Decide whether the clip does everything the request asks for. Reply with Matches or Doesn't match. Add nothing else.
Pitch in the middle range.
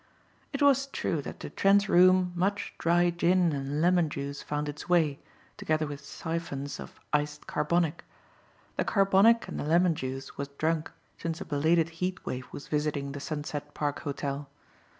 Matches